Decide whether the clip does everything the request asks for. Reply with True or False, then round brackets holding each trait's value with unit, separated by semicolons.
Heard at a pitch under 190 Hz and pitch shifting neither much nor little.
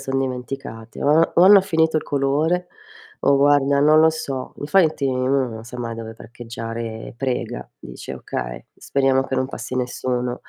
True (135 Hz; 3.2 semitones)